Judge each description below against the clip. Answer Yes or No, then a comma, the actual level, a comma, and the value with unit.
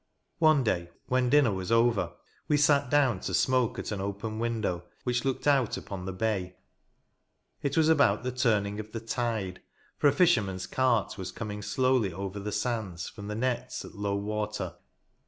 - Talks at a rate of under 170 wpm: No, average, 175 wpm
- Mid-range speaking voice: No, low, 110 Hz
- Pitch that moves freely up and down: No, average, 4.3 semitones